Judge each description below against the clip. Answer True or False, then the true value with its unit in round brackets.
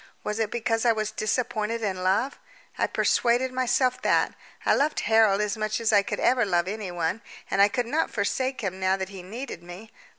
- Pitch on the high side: True (215 Hz)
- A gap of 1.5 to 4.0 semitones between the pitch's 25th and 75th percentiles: True (3.6 semitones)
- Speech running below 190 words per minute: False (200 wpm)